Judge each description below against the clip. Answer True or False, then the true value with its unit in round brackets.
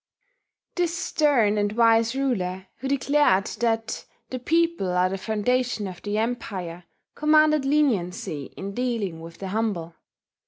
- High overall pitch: True (225 Hz)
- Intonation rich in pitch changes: True (6.0 semitones)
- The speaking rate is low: True (130 wpm)